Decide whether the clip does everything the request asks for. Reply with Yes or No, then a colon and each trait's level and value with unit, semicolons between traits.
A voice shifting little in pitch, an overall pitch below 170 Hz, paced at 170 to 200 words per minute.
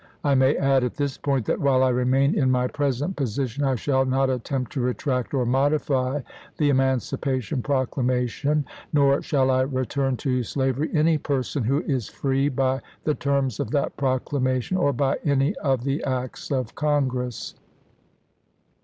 No: narrow, 1.8 semitones; low, 135 Hz; average, 160 wpm